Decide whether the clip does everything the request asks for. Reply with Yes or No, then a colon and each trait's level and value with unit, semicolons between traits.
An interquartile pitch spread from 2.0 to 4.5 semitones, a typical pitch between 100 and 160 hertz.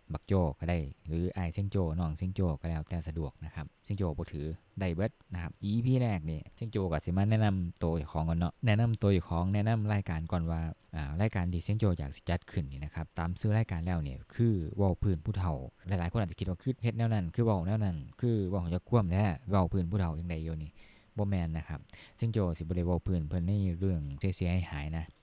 No: average, 3.7 semitones; very low, 90 Hz